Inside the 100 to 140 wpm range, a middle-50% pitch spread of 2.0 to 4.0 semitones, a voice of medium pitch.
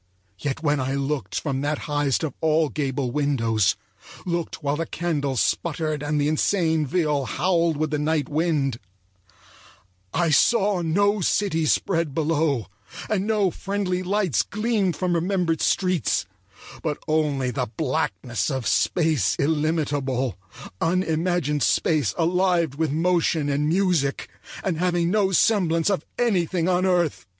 Yes: slow, 135 wpm; average, 3.7 semitones; medium, 160 Hz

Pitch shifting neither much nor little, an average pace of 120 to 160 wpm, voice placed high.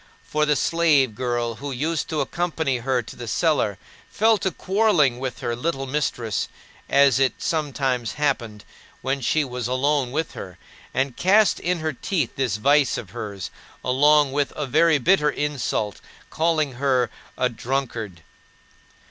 No: average, 3.9 semitones; average, 150 wpm; low, 135 Hz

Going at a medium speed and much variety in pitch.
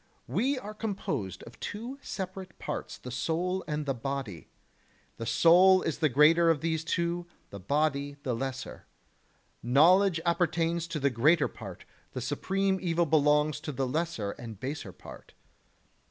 No: average, 155 wpm; average, 4.6 semitones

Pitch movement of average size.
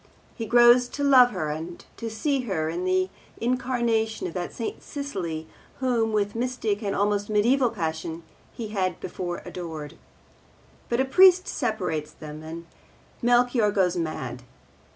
No: wide, 6.1 semitones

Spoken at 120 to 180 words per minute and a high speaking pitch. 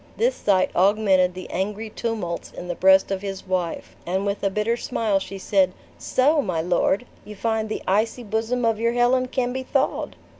No: average, 190 wpm; high, 210 Hz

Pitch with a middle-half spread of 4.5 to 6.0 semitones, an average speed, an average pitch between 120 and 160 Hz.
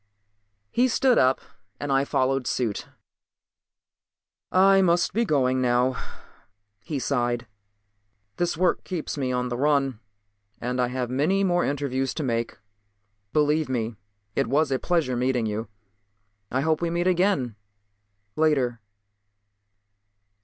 No: average, 4.9 semitones; slow, 125 wpm; low, 135 Hz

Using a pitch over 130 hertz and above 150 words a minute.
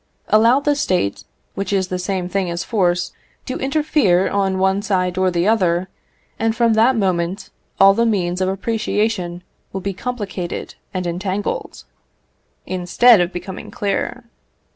No: high, 190 Hz; average, 145 wpm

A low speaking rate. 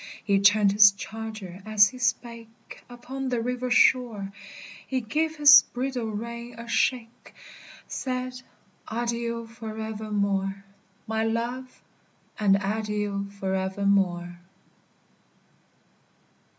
Yes: slow, 100 wpm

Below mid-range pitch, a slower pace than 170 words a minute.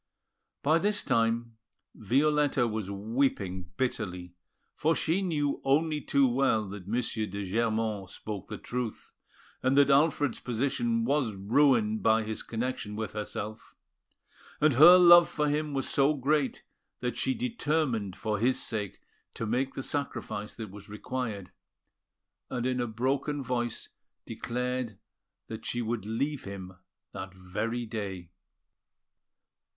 Yes: low, 120 Hz; slow, 135 wpm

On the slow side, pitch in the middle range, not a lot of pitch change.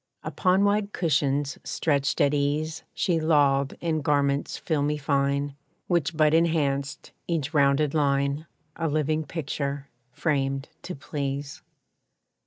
Yes: slow, 115 wpm; medium, 145 Hz; narrow, 2.2 semitones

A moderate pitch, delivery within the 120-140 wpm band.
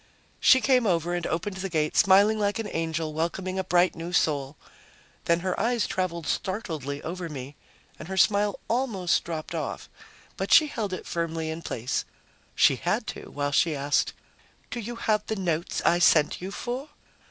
No: medium, 175 Hz; average, 175 wpm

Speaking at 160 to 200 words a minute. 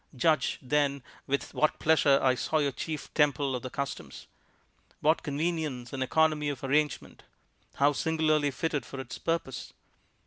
No: average, 145 wpm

